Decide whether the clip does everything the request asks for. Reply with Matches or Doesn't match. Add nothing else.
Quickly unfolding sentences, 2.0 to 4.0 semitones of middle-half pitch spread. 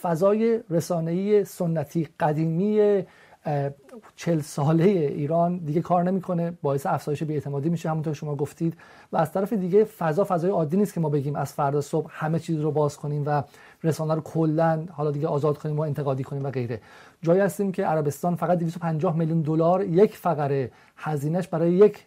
Matches